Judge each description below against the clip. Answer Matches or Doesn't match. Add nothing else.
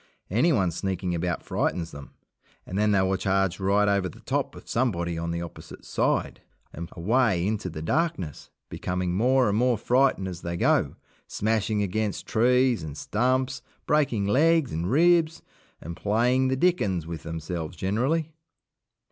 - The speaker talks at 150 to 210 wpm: Matches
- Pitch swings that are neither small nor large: Doesn't match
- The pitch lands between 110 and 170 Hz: Doesn't match